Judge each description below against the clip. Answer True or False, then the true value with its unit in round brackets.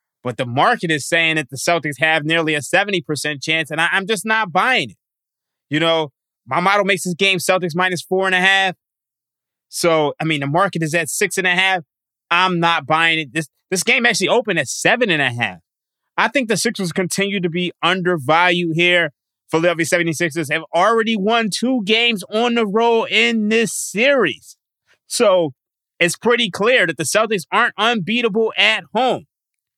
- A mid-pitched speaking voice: True (180 Hz)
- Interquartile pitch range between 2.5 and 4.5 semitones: False (5.2 semitones)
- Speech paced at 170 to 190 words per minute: True (180 wpm)